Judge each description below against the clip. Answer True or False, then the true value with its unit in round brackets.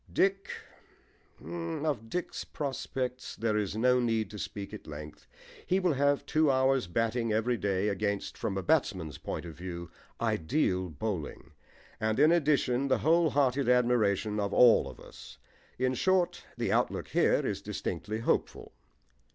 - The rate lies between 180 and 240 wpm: False (150 wpm)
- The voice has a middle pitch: False (115 Hz)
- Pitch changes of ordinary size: False (5.7 semitones)